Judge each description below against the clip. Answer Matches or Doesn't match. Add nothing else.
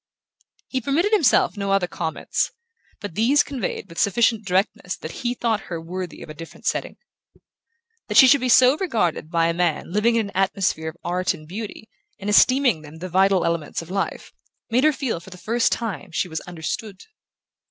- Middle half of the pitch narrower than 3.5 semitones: Doesn't match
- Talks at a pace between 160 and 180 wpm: Doesn't match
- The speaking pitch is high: Matches